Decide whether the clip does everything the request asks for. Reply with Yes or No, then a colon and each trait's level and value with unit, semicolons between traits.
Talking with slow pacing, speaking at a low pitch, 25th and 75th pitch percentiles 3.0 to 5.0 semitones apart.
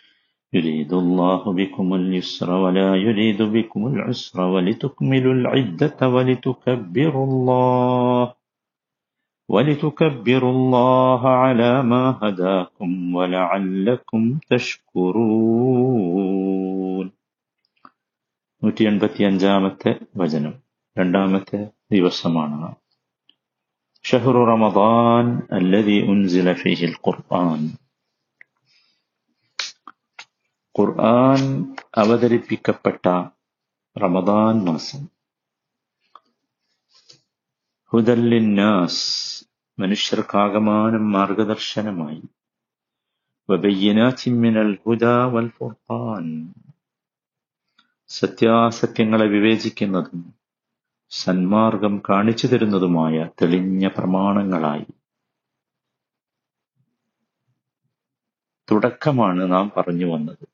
Yes: slow, 45 wpm; low, 105 Hz; average, 4.5 semitones